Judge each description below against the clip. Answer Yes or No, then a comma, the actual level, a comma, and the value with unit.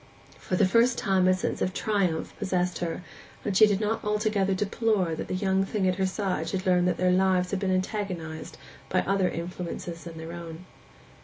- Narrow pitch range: Yes, narrow, 1.9 semitones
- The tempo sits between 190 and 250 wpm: Yes, average, 200 wpm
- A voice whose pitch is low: No, medium, 185 Hz